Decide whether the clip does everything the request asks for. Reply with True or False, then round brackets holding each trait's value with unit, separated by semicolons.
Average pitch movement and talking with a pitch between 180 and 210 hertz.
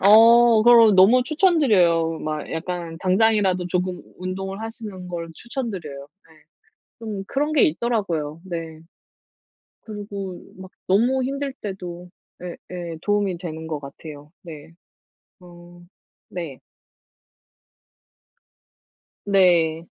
True (4.6 semitones; 185 Hz)